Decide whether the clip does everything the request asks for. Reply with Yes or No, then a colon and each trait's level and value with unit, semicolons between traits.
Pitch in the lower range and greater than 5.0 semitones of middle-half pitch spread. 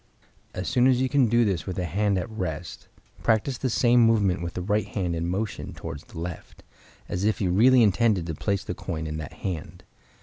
No: low, 100 Hz; average, 4.6 semitones